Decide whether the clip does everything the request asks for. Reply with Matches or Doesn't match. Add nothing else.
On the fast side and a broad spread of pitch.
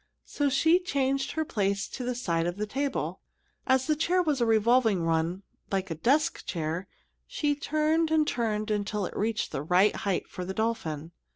Doesn't match